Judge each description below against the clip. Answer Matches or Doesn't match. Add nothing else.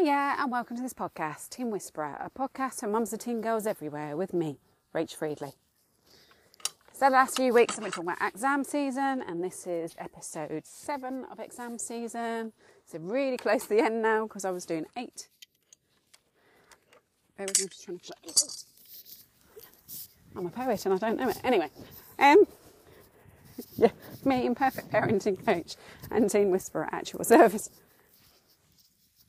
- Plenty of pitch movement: Matches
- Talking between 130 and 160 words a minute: Matches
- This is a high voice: Matches